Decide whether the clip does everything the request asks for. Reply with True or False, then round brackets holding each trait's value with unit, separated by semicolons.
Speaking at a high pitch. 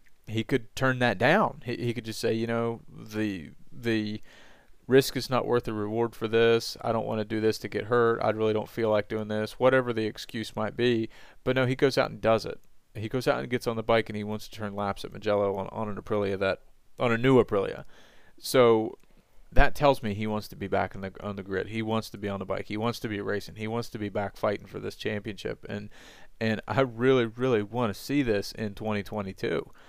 False (110 Hz)